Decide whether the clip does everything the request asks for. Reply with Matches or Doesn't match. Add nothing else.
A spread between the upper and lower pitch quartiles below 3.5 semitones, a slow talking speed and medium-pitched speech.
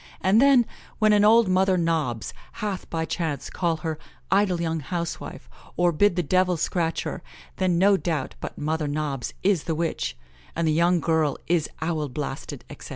Doesn't match